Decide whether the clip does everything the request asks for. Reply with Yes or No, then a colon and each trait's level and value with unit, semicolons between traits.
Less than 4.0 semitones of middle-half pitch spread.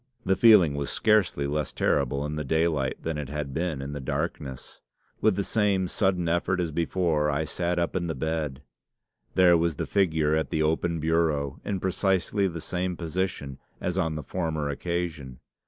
Yes: average, 3.4 semitones